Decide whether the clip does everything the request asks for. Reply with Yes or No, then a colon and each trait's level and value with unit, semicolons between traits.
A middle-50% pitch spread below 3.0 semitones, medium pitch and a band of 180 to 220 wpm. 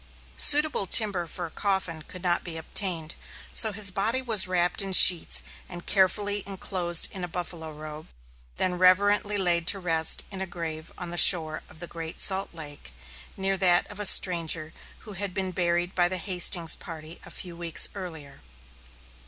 No: narrow, 2.6 semitones; medium, 180 Hz; average, 170 wpm